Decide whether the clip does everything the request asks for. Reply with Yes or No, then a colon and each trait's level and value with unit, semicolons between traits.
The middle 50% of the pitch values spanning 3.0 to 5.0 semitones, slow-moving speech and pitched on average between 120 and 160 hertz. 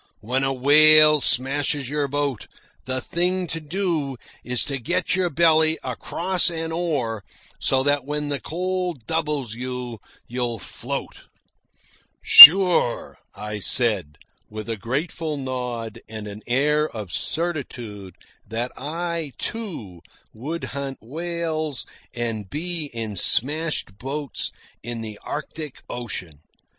No: wide, 5.4 semitones; slow, 120 wpm; medium, 140 Hz